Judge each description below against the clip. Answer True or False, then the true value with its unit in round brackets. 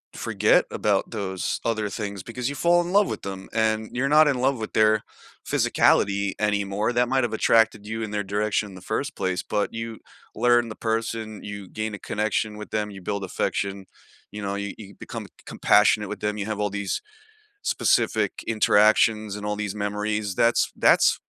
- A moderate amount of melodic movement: False (1.8 semitones)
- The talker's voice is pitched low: True (105 Hz)